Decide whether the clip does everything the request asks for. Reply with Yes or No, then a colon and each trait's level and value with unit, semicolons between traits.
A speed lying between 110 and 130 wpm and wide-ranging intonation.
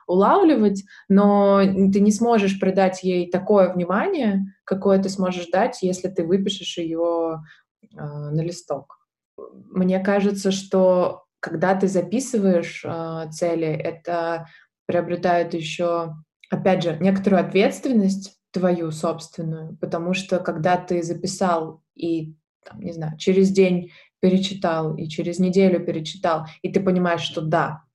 No: average, 125 wpm; narrow, 2.5 semitones